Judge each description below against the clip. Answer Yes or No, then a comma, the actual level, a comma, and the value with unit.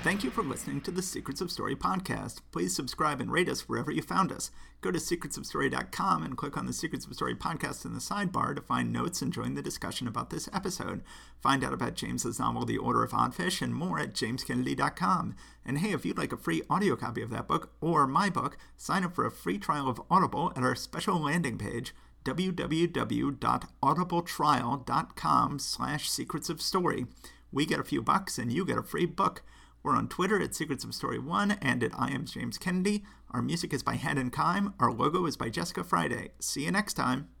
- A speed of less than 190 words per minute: No, fast, 205 wpm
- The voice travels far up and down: Yes, wide, 6.3 semitones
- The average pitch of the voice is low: No, medium, 145 Hz